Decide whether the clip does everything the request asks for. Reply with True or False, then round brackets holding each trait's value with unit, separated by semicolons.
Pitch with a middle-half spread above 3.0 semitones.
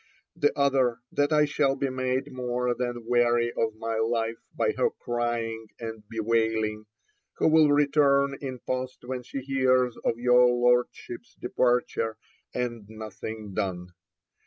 False (2.5 semitones)